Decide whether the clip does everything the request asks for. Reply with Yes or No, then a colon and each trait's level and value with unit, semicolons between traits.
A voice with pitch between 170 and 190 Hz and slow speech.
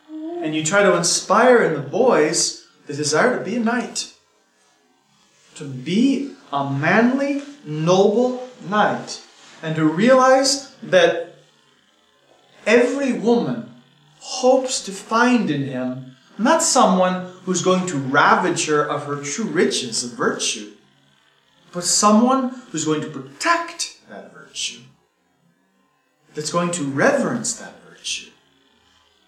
Yes: medium, 185 Hz; slow, 120 wpm